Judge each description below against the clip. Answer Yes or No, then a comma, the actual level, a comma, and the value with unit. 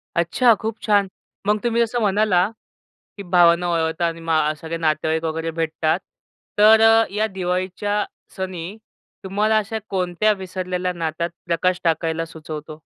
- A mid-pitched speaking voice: Yes, medium, 180 Hz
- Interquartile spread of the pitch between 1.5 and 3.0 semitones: No, average, 3.9 semitones